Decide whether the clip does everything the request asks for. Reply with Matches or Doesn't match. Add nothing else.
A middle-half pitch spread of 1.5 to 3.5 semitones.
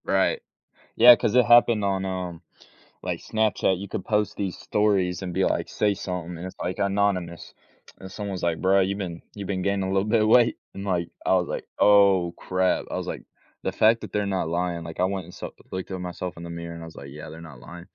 Matches